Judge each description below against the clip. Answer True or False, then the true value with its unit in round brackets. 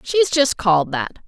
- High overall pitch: True (220 Hz)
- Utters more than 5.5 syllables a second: False (4.5 syllables/s)